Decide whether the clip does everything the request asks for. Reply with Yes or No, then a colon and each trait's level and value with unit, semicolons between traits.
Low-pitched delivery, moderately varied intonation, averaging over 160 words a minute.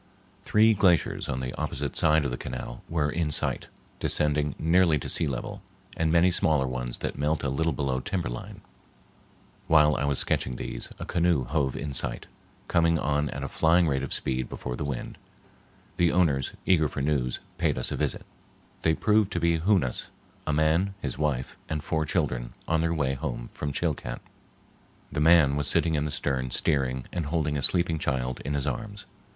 Yes: very low, 75 Hz; average, 3.7 semitones; average, 190 wpm